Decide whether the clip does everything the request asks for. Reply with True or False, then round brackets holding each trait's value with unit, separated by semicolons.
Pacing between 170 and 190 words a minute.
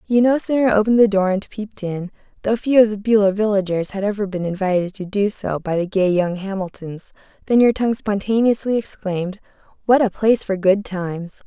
False (200 wpm)